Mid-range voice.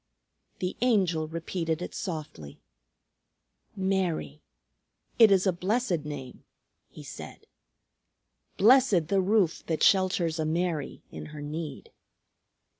Yes: medium, 175 Hz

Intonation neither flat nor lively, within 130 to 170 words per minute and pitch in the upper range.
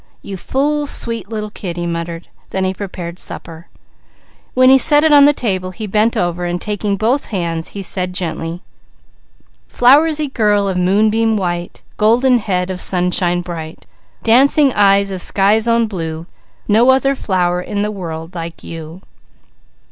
Yes: average, 4.6 semitones; average, 155 wpm; high, 195 Hz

